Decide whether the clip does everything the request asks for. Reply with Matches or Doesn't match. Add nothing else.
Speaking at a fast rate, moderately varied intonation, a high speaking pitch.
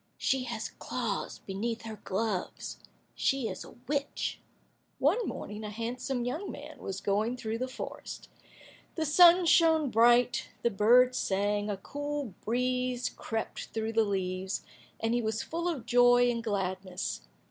Doesn't match